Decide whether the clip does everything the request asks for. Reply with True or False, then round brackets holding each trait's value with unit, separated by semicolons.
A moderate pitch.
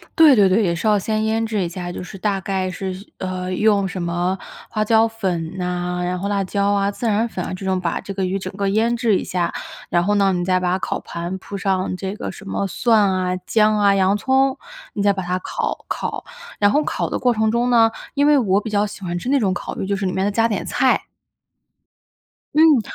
False (195 Hz)